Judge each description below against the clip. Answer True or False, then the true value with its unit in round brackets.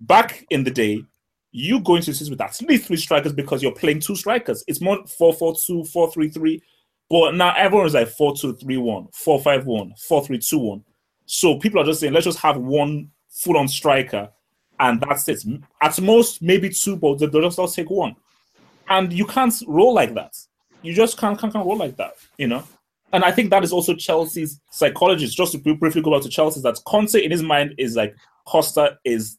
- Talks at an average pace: False (215 wpm)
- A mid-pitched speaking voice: True (160 Hz)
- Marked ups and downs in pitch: False (4.7 semitones)